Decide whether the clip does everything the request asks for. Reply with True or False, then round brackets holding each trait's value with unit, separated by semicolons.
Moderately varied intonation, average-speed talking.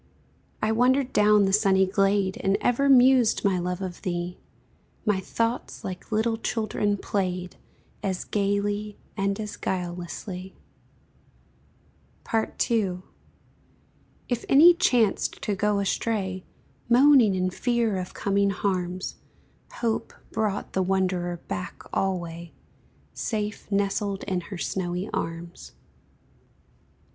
False (3.0 semitones; 110 wpm)